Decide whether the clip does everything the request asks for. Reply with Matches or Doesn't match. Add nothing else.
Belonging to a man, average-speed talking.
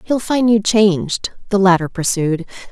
Doesn't match